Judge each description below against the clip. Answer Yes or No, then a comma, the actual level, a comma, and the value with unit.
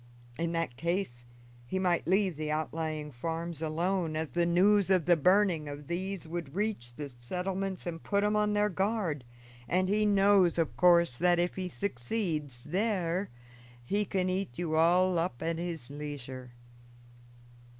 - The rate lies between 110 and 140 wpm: No, average, 160 wpm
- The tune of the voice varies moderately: Yes, average, 3.7 semitones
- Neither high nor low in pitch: Yes, medium, 175 Hz